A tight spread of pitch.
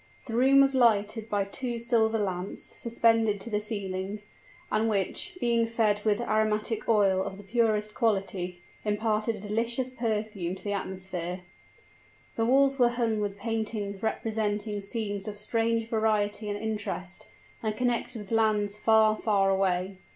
Yes: narrow, 2.1 semitones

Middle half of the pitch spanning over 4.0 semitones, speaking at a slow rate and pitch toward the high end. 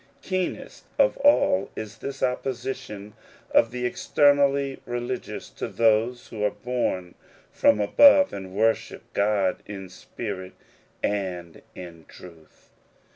No: average, 5.0 semitones; slow, 115 wpm; low, 110 Hz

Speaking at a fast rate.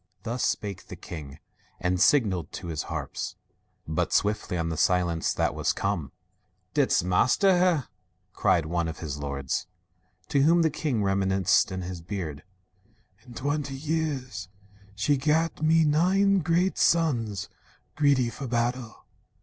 No: average, 140 wpm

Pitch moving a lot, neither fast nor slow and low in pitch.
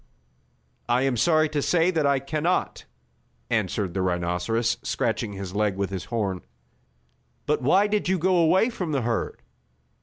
Yes: wide, 8.2 semitones; average, 160 wpm; low, 130 Hz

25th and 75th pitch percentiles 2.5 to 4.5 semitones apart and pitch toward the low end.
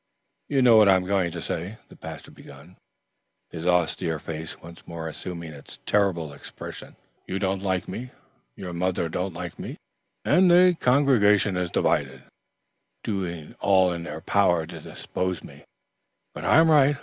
Yes: average, 3.5 semitones; very low, 90 Hz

